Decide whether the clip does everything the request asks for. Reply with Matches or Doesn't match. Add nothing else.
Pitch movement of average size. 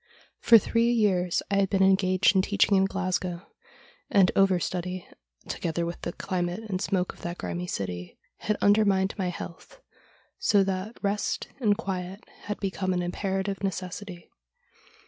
Doesn't match